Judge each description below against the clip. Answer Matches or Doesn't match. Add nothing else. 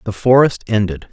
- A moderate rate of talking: Matches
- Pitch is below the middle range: Matches